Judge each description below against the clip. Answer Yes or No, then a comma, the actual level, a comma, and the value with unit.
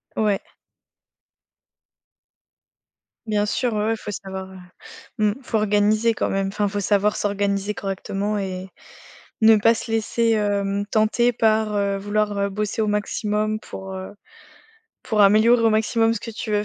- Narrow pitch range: Yes, narrow, 1.6 semitones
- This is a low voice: No, high, 210 Hz